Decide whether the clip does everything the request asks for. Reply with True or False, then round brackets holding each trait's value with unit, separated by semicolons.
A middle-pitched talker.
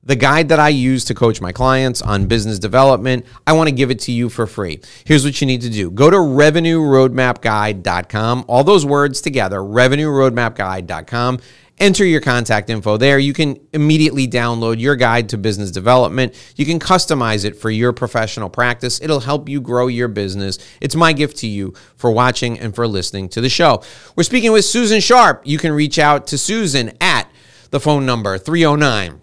False (125 Hz)